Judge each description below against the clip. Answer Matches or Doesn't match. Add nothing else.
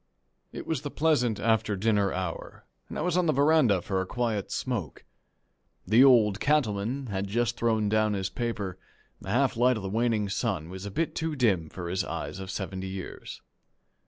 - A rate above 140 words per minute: Matches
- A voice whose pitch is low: Matches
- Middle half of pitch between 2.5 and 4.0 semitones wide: Doesn't match